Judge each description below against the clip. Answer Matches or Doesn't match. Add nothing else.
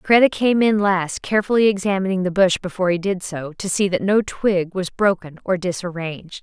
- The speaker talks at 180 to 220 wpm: Matches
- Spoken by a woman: Matches